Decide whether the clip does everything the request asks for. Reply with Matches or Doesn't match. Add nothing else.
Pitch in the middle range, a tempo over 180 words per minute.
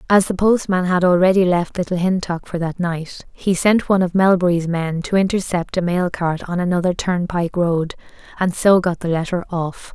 Matches